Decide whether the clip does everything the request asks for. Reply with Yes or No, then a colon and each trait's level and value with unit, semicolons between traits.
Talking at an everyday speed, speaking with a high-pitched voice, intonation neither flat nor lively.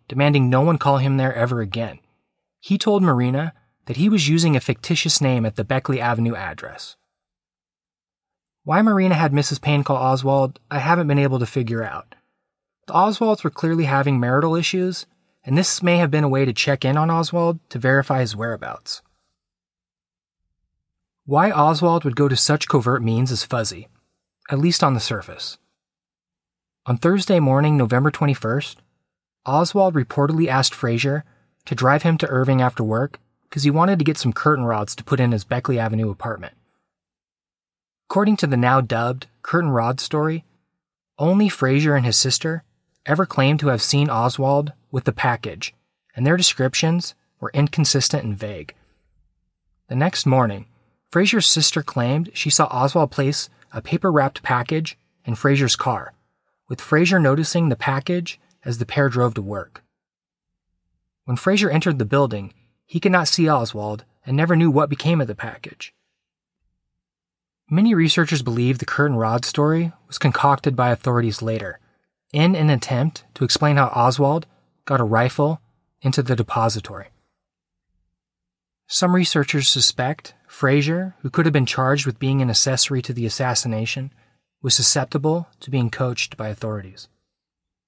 No: average, 155 wpm; low, 135 Hz; average, 4.9 semitones